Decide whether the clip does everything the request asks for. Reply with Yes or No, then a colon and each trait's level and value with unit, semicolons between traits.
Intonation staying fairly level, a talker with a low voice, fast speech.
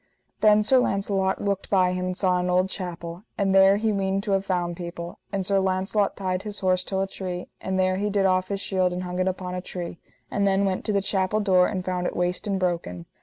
No: narrow, 1.5 semitones; high, 190 Hz; fast, 245 wpm